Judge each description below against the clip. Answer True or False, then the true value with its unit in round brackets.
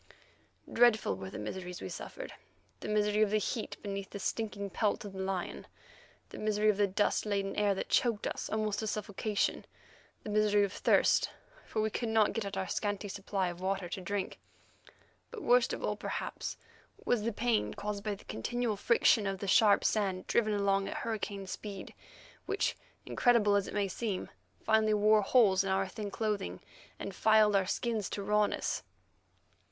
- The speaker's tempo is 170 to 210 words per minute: True (180 wpm)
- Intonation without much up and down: True (1.7 semitones)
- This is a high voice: True (205 Hz)